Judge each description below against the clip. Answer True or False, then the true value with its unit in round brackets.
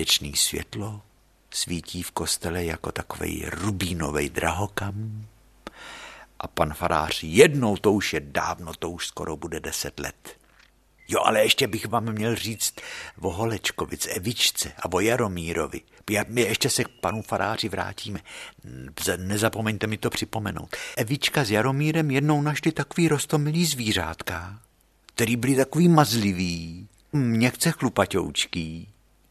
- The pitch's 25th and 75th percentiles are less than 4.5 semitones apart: False (5.1 semitones)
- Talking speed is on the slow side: False (125 wpm)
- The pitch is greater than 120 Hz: False (110 Hz)